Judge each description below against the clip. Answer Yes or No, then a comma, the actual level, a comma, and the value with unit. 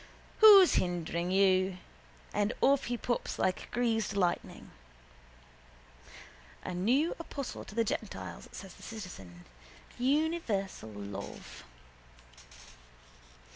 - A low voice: No, high, 200 Hz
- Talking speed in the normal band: No, slow, 95 wpm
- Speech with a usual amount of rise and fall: No, wide, 5.7 semitones